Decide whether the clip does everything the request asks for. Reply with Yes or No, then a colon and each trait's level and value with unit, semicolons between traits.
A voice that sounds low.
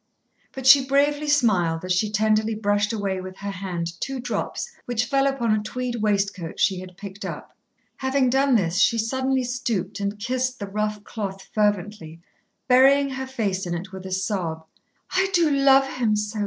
No: high, 215 Hz